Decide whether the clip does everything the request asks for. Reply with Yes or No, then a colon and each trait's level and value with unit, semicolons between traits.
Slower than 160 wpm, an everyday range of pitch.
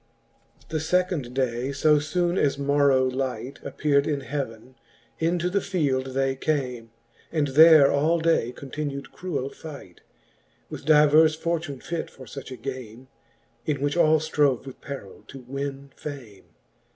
Yes: average, 145 wpm; average, 3.0 semitones